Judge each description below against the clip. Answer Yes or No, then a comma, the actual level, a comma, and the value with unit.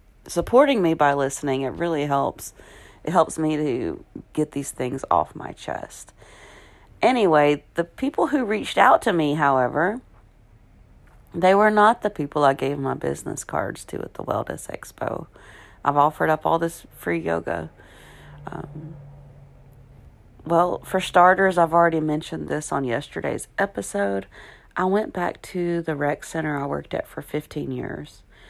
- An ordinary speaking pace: Yes, average, 150 wpm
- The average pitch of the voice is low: No, medium, 150 Hz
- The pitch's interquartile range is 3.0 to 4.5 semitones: Yes, average, 3.8 semitones